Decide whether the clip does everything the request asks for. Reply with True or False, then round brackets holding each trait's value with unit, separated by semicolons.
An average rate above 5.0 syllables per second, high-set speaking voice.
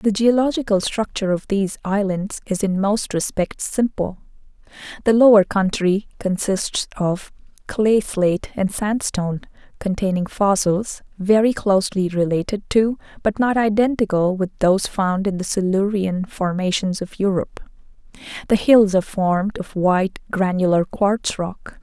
False (4.6 syllables/s; 200 Hz)